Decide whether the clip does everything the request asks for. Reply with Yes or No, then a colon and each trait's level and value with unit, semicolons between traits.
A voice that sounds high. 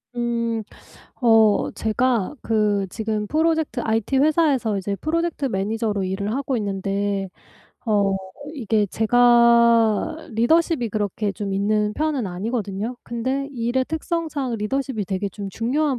Yes: high, 225 Hz